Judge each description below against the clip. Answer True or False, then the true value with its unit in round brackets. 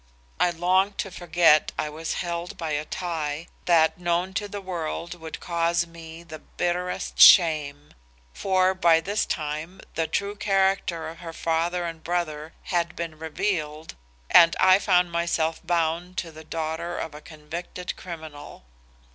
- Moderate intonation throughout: False (2.0 semitones)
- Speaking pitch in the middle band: True (170 Hz)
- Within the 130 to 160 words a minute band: True (150 wpm)